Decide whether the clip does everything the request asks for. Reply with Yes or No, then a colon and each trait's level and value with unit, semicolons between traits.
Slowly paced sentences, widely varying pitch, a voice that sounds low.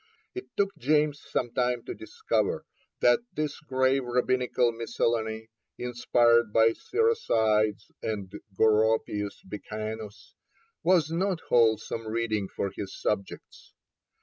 No: slow, 105 wpm; average, 4.0 semitones; low, 115 Hz